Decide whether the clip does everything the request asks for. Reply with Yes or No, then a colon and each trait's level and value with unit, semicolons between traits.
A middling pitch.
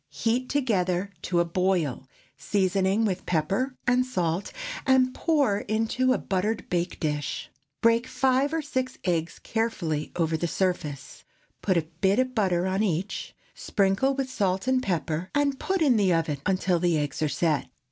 No: high, 195 Hz